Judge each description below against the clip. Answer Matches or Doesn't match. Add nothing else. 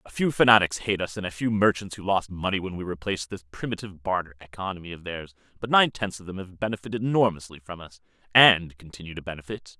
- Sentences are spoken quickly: Matches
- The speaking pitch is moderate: Doesn't match